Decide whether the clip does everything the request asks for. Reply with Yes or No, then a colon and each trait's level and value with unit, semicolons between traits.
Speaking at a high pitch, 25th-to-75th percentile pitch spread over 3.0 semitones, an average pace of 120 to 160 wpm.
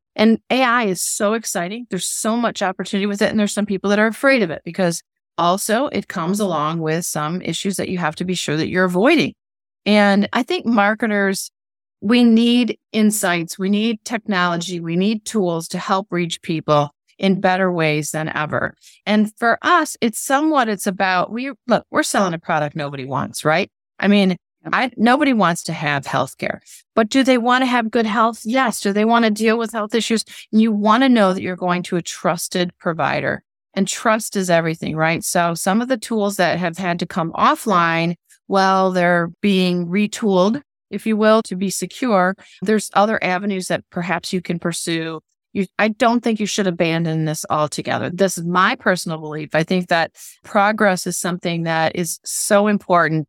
No: high, 195 Hz; average, 4.0 semitones; average, 190 wpm